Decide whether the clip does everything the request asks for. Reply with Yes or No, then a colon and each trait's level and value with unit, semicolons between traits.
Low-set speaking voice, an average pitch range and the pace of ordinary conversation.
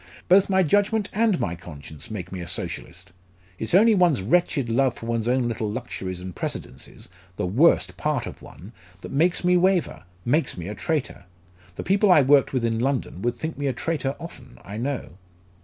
No: low, 130 Hz; wide, 8.0 semitones; average, 190 wpm